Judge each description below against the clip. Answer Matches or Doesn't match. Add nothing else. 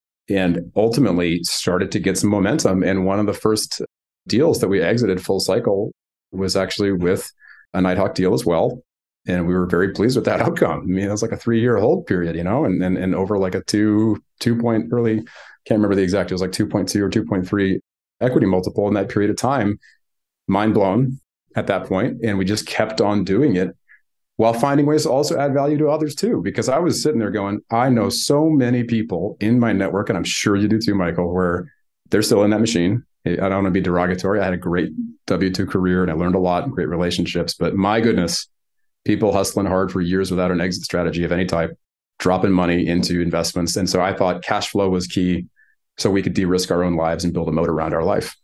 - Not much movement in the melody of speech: Doesn't match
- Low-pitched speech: Matches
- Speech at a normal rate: Doesn't match